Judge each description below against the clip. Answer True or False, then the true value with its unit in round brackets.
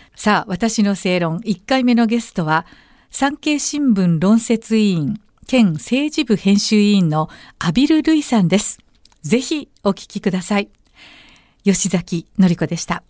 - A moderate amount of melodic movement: True (4.6 semitones)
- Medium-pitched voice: False (205 Hz)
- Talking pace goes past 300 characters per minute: False (255 characters per minute)